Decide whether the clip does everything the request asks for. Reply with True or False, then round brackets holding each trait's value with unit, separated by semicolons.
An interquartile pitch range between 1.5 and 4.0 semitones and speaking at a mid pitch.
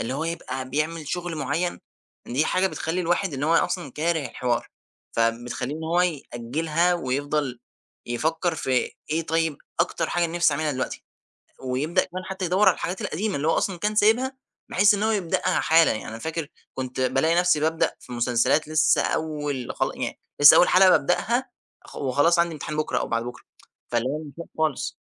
False (4.7 semitones; 160 Hz)